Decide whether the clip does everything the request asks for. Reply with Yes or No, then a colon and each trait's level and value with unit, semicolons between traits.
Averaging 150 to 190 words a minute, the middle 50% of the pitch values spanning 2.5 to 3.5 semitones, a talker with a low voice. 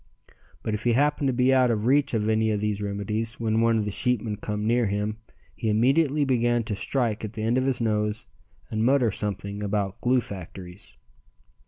No: average, 200 wpm; average, 2.9 semitones; low, 110 Hz